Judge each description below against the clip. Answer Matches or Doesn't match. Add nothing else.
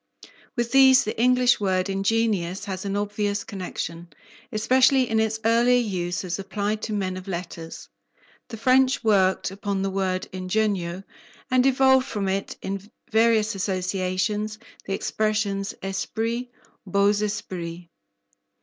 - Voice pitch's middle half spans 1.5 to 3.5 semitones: Matches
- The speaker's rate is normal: Doesn't match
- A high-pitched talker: Matches